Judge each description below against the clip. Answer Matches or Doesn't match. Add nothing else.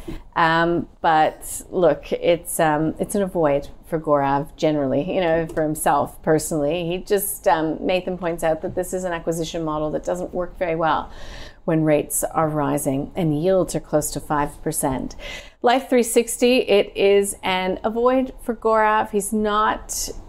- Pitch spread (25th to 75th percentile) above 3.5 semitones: Matches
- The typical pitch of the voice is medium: Matches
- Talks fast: Doesn't match